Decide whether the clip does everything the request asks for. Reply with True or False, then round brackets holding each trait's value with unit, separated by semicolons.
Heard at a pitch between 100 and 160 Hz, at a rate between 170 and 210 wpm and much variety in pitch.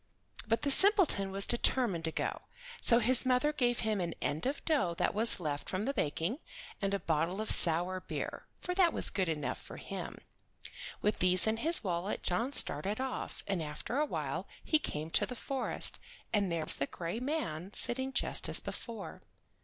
False (210 Hz; 185 wpm; 7.0 semitones)